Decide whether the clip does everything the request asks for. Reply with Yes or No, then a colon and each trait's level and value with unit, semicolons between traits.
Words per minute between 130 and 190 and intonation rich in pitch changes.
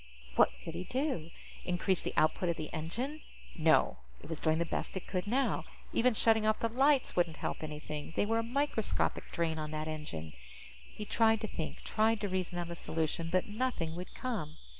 No: average, 200 wpm; wide, 6.0 semitones